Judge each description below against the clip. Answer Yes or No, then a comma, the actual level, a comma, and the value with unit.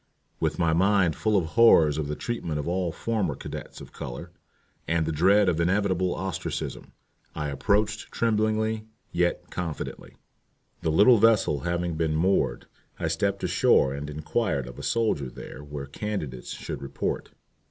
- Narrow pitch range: No, wide, 5.5 semitones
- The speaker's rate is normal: Yes, average, 155 wpm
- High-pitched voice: No, very low, 85 Hz